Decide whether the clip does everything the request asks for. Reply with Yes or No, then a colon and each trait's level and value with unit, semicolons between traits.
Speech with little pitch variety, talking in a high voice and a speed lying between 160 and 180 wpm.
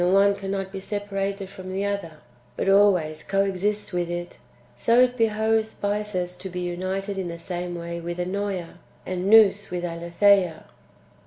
Yes: narrow, 2.3 semitones; high, 195 Hz; average, 165 wpm